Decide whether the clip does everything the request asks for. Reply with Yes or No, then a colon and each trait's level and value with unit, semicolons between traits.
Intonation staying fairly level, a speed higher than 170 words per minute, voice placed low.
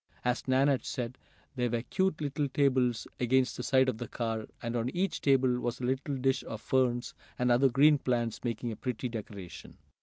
Yes: narrow, 2.0 semitones; average, 195 wpm; low, 125 Hz